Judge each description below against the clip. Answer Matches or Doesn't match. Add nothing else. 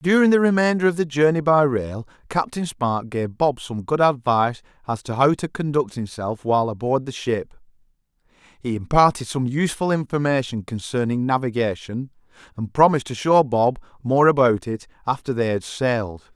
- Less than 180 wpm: Matches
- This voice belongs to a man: Matches